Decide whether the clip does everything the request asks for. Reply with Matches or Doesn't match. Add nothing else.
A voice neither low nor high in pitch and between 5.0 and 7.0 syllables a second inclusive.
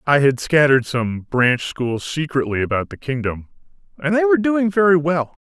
Matches